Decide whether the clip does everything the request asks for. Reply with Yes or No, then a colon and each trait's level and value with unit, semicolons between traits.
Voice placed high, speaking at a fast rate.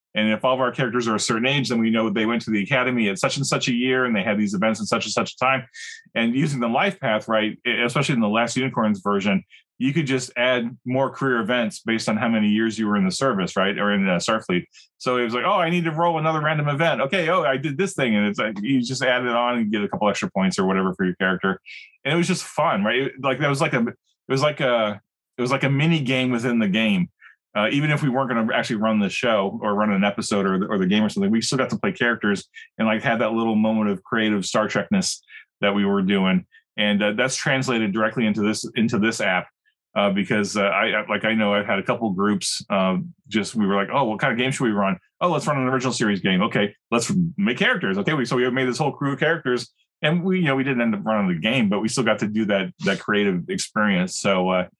No: low, 120 Hz; fast, 275 wpm